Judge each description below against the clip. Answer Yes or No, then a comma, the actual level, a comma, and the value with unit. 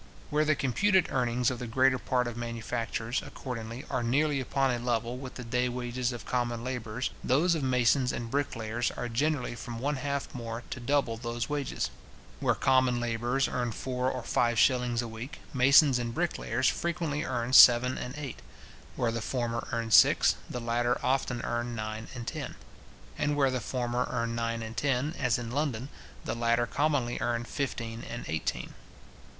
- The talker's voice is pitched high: No, low, 125 Hz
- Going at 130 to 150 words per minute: No, average, 175 wpm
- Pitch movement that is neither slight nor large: No, narrow, 2.1 semitones